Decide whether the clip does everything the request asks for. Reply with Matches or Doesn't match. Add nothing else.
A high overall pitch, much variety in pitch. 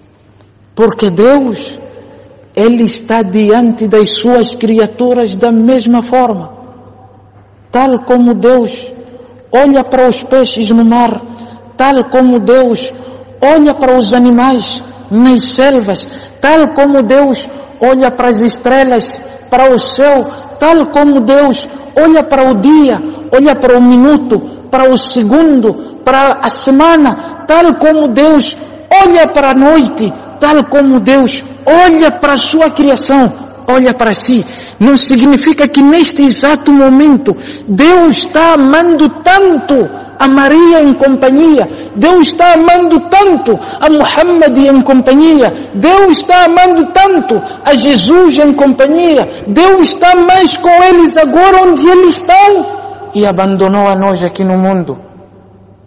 Doesn't match